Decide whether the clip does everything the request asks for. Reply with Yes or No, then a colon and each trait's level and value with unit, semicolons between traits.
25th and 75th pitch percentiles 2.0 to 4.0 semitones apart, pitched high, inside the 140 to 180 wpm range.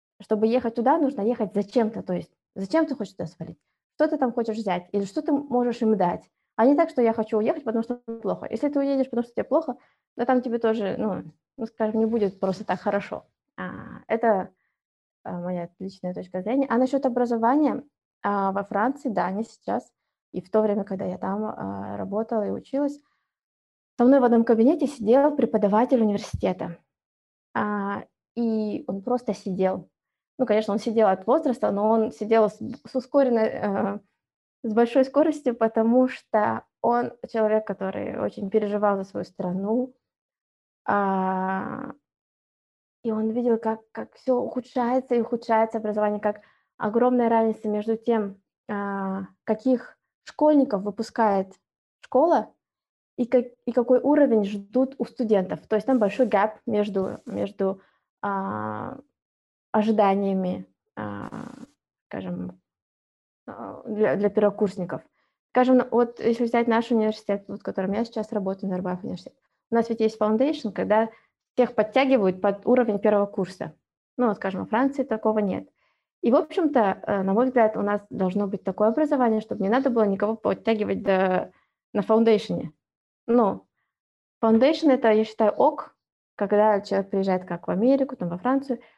Yes: average, 3.6 semitones; high, 220 Hz; average, 150 wpm